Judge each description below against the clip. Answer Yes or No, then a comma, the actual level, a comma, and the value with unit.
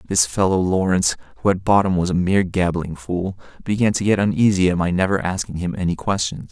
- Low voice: Yes, very low, 90 Hz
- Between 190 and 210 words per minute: Yes, fast, 205 wpm